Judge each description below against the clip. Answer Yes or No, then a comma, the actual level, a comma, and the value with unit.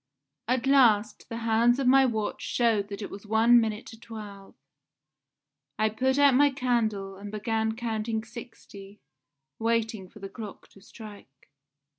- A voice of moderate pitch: No, high, 220 Hz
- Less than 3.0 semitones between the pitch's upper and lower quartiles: Yes, narrow, 2.4 semitones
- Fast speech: No, average, 150 wpm